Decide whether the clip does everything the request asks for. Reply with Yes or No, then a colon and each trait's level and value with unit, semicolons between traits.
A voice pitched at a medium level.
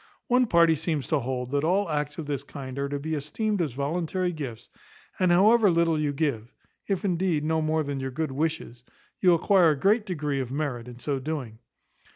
Yes: medium, 155 Hz